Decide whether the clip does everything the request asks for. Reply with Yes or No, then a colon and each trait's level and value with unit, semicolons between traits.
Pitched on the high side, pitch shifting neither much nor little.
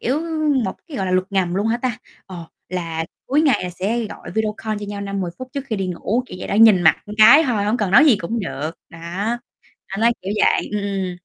Yes: high, 205 Hz; average, 3.7 semitones